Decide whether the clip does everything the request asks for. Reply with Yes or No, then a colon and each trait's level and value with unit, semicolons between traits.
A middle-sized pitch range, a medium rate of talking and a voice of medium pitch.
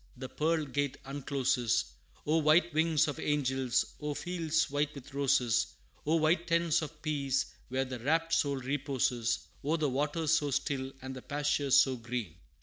Yes: average, 3.0 semitones; average, 160 wpm; medium, 145 Hz